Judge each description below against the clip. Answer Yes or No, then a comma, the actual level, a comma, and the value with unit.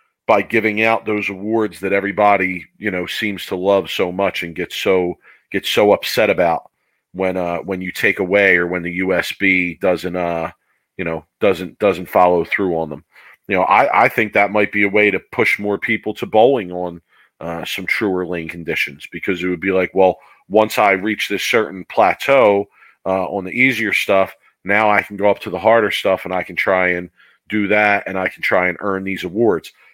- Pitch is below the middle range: Yes, very low, 95 Hz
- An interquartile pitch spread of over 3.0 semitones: No, narrow, 2.4 semitones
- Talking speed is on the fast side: Yes, fast, 210 wpm